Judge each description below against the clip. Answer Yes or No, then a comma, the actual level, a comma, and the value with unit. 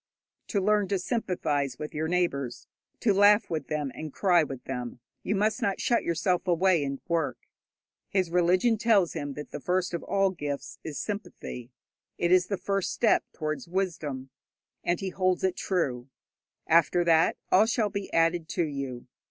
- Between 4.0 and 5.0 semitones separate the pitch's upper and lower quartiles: Yes, average, 4.6 semitones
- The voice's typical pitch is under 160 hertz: No, medium, 175 Hz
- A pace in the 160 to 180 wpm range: Yes, average, 170 wpm